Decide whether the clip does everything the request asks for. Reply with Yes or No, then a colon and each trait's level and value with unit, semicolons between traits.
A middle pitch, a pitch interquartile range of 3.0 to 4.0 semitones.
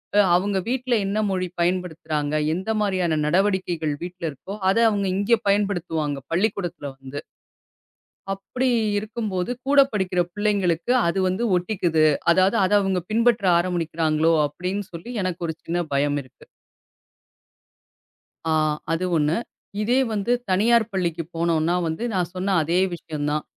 Yes: medium, 180 Hz; average, 3.7 semitones